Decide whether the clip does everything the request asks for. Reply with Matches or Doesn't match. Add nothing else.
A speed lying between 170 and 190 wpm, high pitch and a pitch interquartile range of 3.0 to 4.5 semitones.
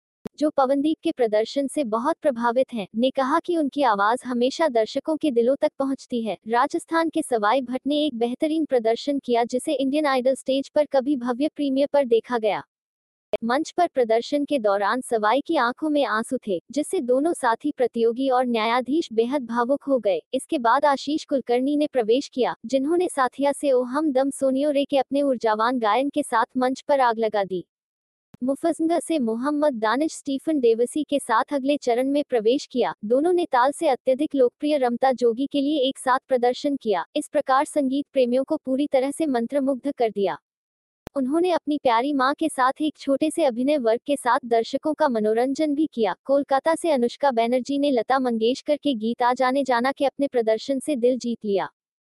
Matches